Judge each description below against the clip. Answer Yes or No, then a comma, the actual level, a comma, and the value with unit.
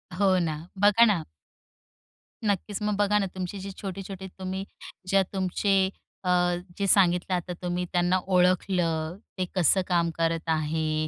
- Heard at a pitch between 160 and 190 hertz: Yes, medium, 185 Hz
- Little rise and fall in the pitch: Yes, narrow, 2.2 semitones